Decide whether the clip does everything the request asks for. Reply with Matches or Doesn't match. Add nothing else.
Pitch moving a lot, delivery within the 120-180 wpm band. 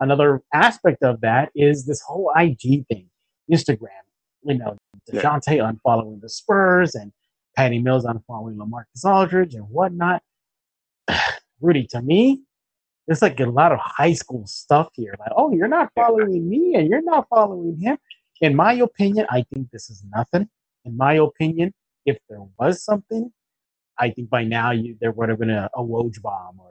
Matches